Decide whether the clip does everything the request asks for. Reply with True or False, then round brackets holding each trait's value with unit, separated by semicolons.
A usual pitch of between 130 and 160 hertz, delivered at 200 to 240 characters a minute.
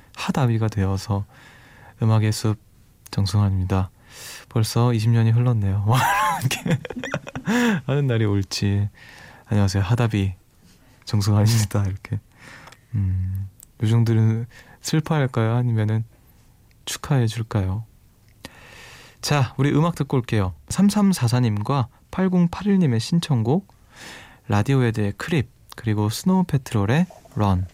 False (115 Hz; 235 characters per minute)